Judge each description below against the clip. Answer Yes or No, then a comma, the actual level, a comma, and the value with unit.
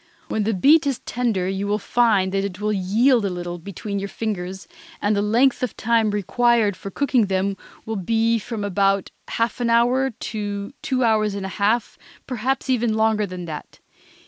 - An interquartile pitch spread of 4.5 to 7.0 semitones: No, average, 3.1 semitones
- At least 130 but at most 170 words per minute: No, average, 180 wpm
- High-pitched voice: Yes, high, 215 Hz